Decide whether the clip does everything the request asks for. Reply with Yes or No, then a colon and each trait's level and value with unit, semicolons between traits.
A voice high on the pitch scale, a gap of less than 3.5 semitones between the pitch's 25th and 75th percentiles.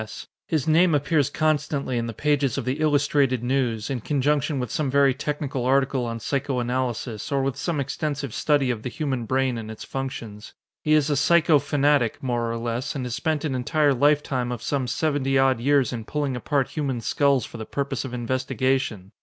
No: low, 135 Hz; average, 2.9 semitones